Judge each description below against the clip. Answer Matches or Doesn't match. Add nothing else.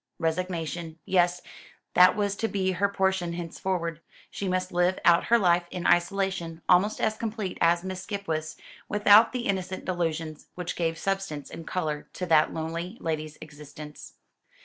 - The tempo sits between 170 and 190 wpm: Doesn't match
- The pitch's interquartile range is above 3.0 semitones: Doesn't match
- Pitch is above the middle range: Doesn't match